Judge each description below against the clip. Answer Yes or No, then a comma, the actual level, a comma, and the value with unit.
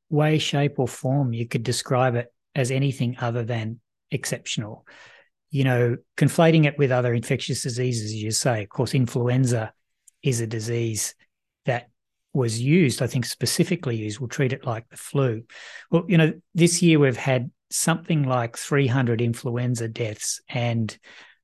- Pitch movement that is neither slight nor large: Yes, average, 3.1 semitones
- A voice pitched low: Yes, low, 125 Hz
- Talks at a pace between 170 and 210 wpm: No, average, 155 wpm